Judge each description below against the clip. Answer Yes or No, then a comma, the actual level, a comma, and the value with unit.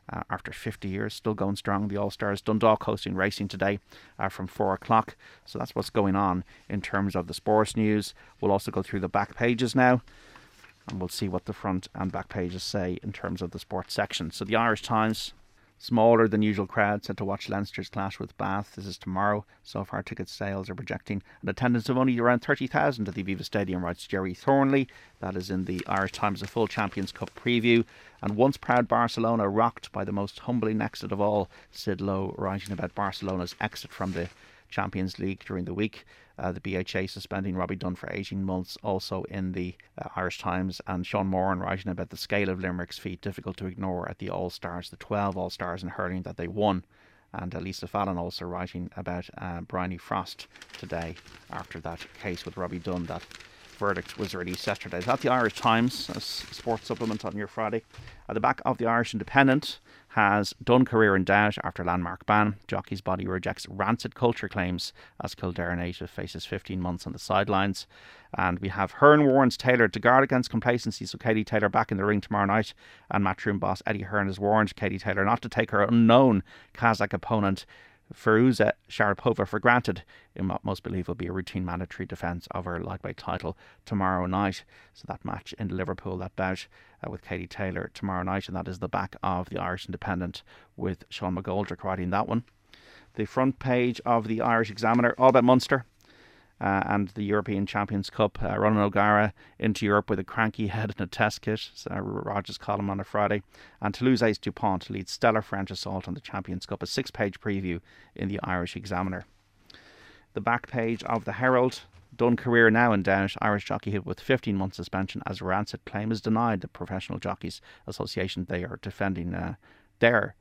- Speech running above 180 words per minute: Yes, average, 200 wpm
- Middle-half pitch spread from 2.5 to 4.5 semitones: Yes, average, 2.9 semitones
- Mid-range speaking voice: No, low, 100 Hz